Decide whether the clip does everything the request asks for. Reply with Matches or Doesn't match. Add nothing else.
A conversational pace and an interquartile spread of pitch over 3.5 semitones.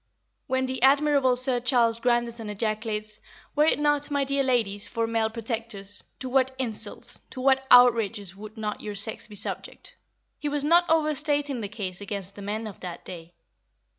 Matches